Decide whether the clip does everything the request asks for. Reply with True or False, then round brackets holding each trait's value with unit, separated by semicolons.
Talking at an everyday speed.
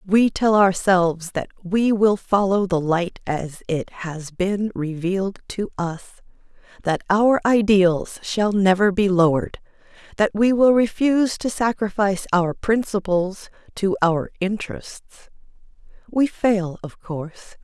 False (130 wpm)